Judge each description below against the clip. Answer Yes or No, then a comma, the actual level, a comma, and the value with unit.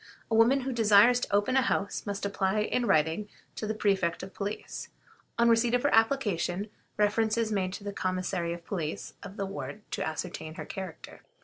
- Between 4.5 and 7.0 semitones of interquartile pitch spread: No, average, 3.3 semitones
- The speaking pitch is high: Yes, high, 205 Hz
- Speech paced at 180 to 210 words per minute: Yes, average, 195 wpm